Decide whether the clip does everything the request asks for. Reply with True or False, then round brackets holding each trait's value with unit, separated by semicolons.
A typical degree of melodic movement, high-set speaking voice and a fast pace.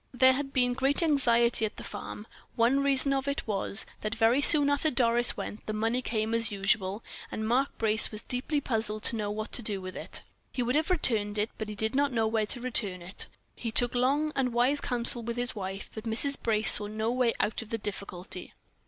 True (3.3 semitones; 230 Hz; 225 wpm)